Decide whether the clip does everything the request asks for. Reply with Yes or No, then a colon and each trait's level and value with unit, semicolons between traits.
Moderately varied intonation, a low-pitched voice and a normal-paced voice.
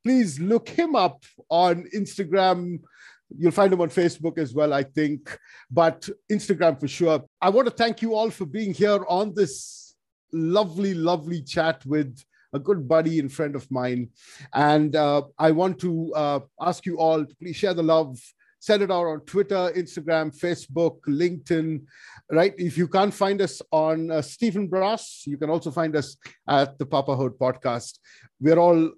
No: average, 4.0 semitones; medium, 165 Hz; average, 175 wpm